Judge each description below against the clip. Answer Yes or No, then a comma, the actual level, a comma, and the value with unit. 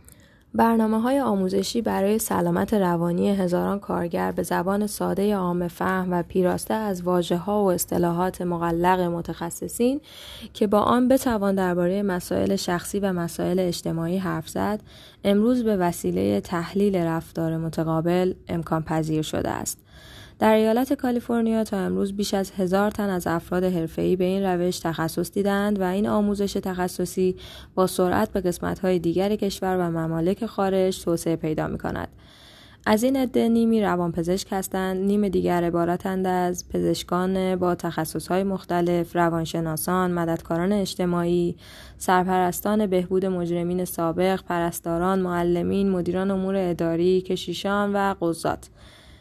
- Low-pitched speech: No, medium, 185 Hz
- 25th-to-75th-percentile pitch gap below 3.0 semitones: Yes, narrow, 2.4 semitones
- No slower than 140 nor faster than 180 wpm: No, average, 130 wpm